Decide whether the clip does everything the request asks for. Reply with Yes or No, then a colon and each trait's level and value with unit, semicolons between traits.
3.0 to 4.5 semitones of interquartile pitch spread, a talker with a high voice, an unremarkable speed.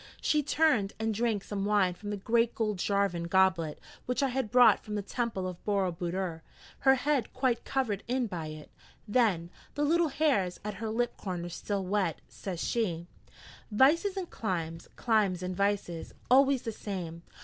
No: average, 5.0 semitones; high, 205 Hz; average, 170 wpm